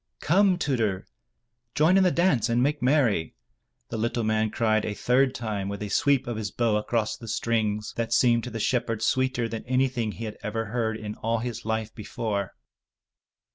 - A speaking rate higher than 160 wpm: Yes, average, 185 wpm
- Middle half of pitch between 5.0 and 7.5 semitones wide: No, average, 2.7 semitones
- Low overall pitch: Yes, low, 115 Hz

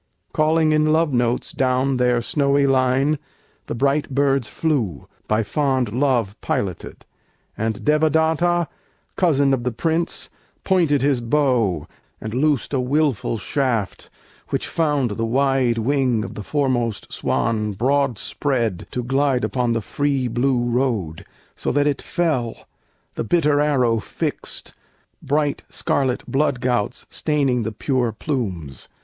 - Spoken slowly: Yes, slow, 130 wpm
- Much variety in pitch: No, average, 3.7 semitones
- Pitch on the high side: No, low, 130 Hz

